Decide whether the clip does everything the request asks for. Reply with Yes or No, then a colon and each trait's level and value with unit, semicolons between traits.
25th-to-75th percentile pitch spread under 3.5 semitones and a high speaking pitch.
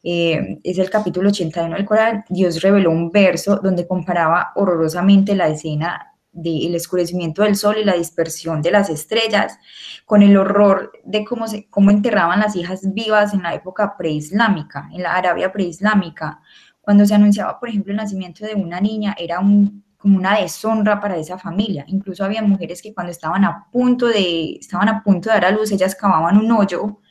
Yes: average, 3.0 semitones; high, 195 Hz